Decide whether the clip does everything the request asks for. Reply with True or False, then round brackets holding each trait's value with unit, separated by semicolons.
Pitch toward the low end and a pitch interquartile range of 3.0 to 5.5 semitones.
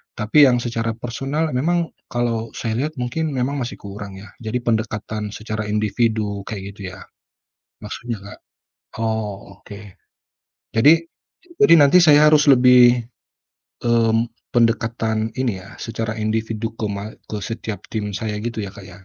False (115 Hz; 2.6 semitones)